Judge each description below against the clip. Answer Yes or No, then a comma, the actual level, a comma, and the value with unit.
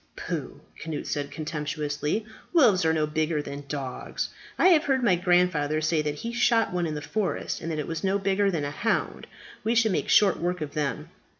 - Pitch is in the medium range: Yes, medium, 165 Hz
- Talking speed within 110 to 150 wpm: No, fast, 205 wpm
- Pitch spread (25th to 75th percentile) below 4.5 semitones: No, average, 5.0 semitones